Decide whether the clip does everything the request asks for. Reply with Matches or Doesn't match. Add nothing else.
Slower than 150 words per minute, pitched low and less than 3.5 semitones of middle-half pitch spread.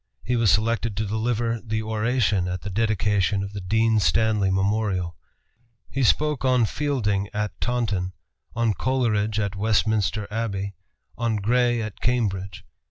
Matches